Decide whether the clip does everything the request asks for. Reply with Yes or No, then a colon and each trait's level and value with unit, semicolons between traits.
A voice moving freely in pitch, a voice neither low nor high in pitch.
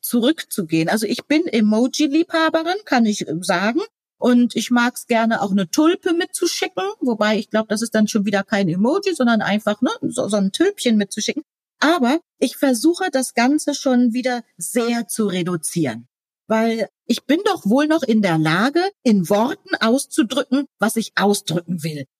No: wide, 6.0 semitones; high, 235 Hz